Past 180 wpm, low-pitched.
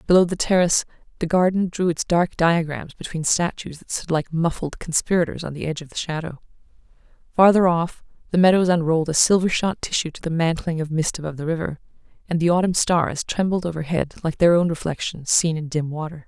No: average, 195 wpm; medium, 165 Hz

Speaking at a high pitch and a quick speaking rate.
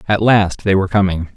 No: very low, 95 Hz; fast, 220 wpm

